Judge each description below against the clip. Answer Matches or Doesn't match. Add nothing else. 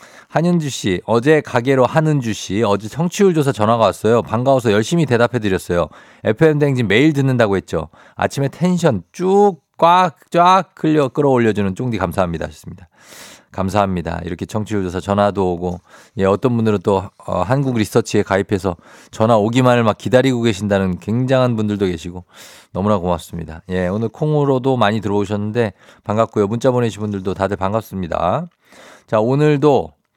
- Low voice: Matches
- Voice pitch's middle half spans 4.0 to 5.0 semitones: Doesn't match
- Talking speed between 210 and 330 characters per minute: Doesn't match